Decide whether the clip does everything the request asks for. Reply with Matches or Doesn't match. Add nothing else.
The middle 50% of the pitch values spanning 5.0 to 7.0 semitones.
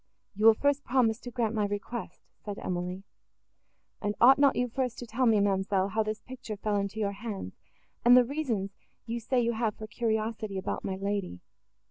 Doesn't match